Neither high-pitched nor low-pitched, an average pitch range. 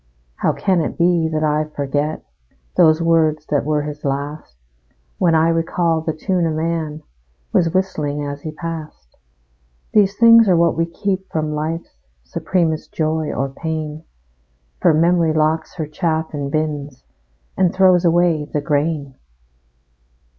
No: medium, 160 Hz; narrow, 2.0 semitones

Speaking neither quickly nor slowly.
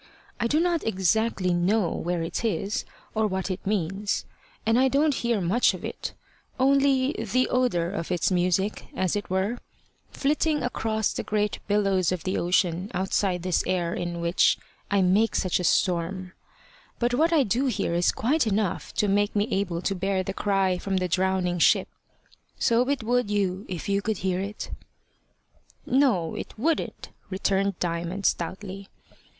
Yes: average, 165 wpm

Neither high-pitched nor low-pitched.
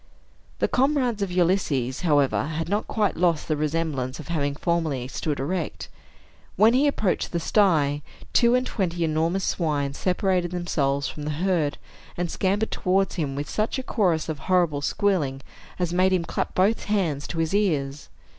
Yes: medium, 170 Hz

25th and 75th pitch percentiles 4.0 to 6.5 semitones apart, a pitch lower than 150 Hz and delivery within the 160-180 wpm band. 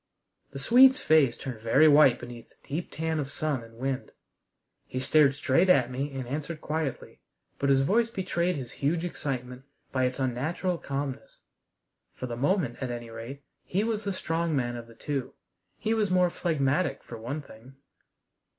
Yes: average, 4.8 semitones; medium, 140 Hz; average, 175 wpm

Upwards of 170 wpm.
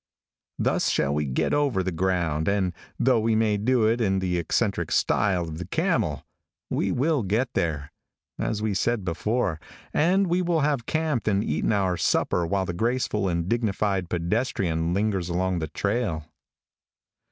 No: average, 165 wpm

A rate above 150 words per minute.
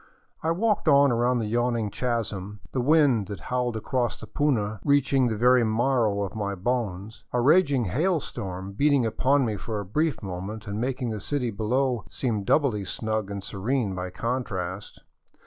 Yes: average, 170 wpm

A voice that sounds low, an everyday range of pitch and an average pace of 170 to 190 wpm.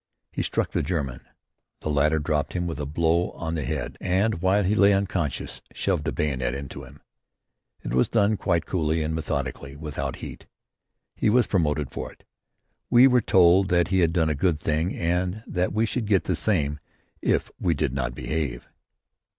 Yes: very low, 80 Hz; average, 4.1 semitones; average, 185 wpm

